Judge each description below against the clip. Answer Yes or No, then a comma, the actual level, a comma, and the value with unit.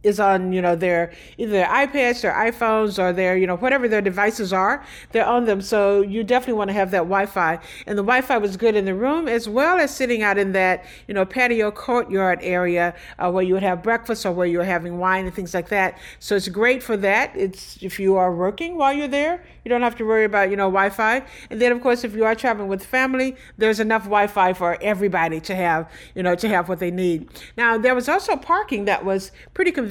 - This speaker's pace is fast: Yes, fast, 240 wpm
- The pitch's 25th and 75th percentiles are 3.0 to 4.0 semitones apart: No, average, 4.4 semitones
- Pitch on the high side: Yes, high, 205 Hz